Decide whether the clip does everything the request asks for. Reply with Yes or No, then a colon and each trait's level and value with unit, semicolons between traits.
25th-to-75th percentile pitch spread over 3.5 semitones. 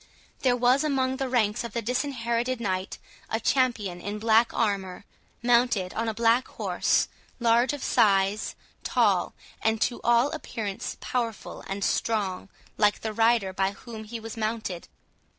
No: average, 2.9 semitones